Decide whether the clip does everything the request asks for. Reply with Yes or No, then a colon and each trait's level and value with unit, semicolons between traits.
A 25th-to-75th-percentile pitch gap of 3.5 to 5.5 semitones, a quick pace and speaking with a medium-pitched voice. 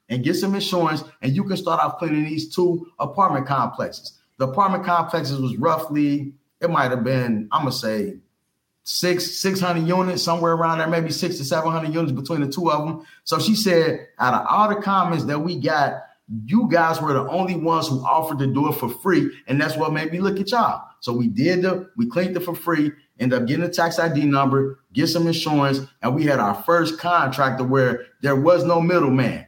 Yes: average, 4.0 semitones; fast, 215 wpm; medium, 160 Hz